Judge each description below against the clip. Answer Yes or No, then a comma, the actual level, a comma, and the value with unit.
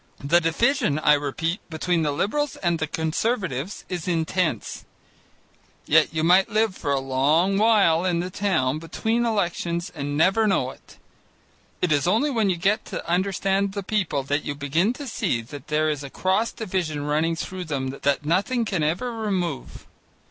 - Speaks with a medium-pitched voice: Yes, medium, 170 Hz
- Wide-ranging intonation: No, average, 4.8 semitones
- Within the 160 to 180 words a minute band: Yes, average, 170 wpm